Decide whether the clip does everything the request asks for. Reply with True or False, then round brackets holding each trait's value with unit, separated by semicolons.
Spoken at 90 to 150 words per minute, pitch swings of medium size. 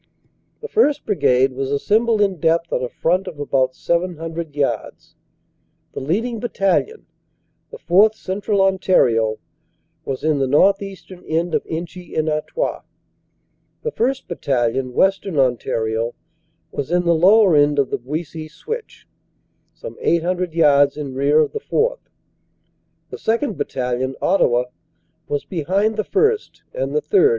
False (140 wpm; 6.5 semitones)